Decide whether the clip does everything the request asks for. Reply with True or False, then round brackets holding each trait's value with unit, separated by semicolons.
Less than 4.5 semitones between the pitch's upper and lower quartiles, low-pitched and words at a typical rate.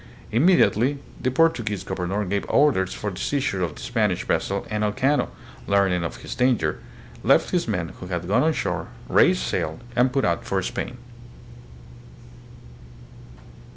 False (5.5 semitones; 105 Hz; 150 wpm)